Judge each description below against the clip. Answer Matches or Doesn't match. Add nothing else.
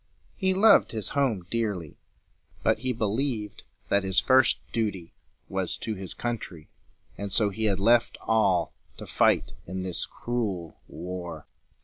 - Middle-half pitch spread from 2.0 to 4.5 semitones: Matches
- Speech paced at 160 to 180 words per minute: Doesn't match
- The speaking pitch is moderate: Doesn't match